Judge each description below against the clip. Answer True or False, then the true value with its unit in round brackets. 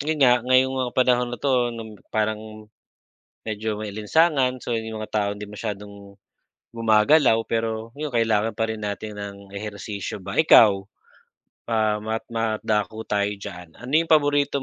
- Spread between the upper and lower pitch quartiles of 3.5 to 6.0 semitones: False (2.9 semitones)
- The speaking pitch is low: True (110 Hz)